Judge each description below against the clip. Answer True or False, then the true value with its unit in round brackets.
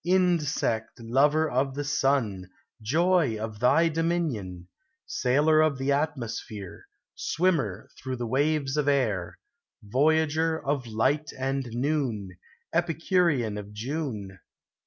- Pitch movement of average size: False (5.8 semitones)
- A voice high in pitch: False (135 Hz)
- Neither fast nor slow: False (110 wpm)